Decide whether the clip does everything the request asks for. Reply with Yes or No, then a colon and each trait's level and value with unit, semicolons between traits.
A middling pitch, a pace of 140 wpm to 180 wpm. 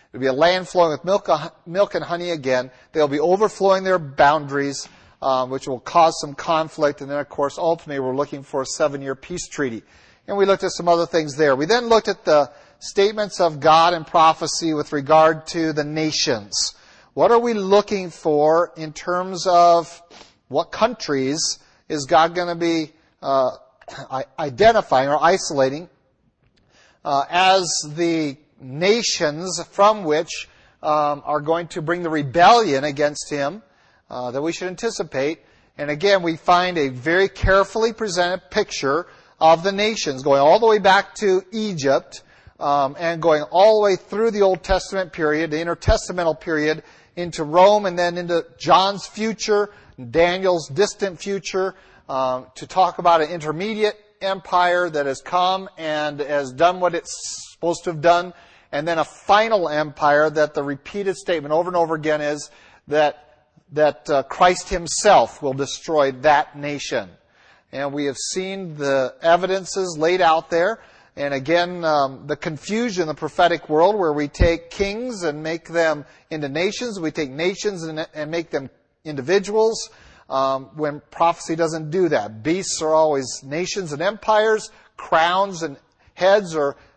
Yes: medium, 165 Hz; average, 160 wpm